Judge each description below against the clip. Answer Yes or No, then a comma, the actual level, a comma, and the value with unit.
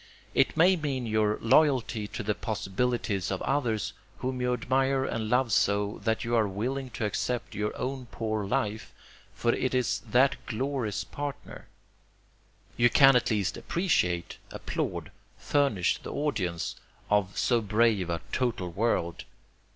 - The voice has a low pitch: Yes, low, 115 Hz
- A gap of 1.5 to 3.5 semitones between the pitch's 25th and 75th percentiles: No, average, 4.0 semitones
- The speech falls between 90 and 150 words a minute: Yes, average, 145 wpm